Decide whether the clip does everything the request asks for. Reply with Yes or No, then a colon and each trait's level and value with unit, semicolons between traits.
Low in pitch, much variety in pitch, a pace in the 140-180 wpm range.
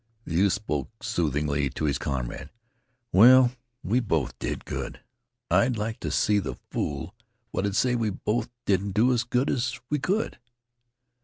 Yes: low, 105 Hz; wide, 7.4 semitones; average, 155 wpm